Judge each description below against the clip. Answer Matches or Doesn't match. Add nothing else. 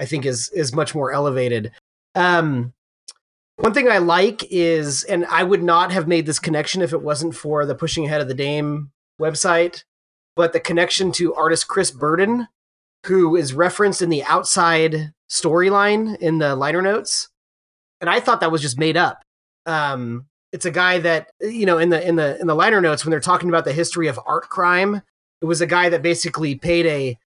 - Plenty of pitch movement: Doesn't match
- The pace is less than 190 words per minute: Doesn't match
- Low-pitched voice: Doesn't match